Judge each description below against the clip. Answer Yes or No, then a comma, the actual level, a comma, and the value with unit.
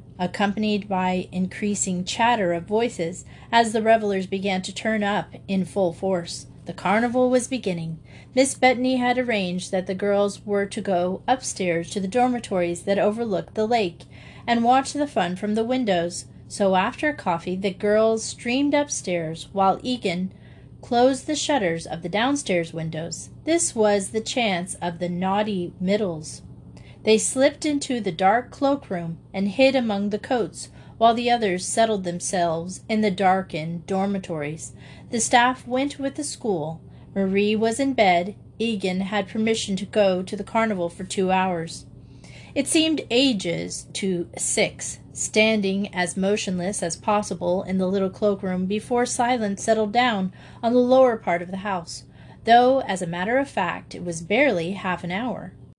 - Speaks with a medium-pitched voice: No, high, 200 Hz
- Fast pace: No, average, 160 wpm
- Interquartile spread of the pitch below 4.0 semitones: No, average, 4.4 semitones